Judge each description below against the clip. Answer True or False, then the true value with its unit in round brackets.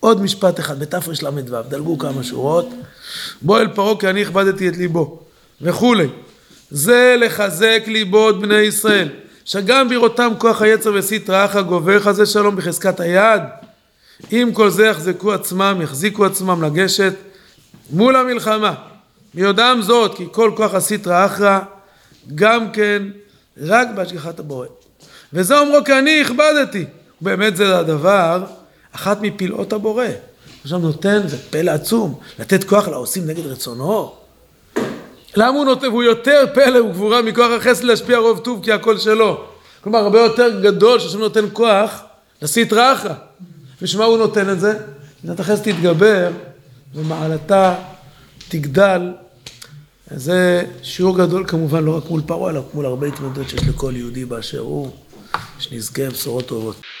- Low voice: False (195 Hz)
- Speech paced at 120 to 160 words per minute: True (140 wpm)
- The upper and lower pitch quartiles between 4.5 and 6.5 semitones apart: True (5.1 semitones)